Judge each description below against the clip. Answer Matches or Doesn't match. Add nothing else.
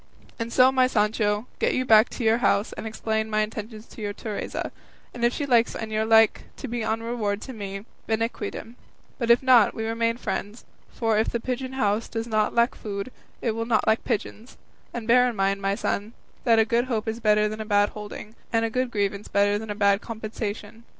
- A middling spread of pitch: Doesn't match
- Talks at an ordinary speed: Doesn't match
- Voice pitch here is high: Matches